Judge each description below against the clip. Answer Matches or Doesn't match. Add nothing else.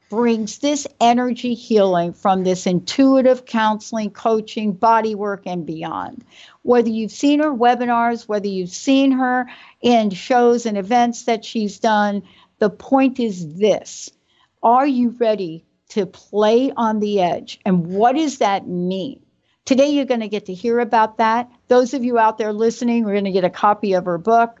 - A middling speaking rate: Matches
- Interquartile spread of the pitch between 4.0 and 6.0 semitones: Doesn't match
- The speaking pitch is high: Matches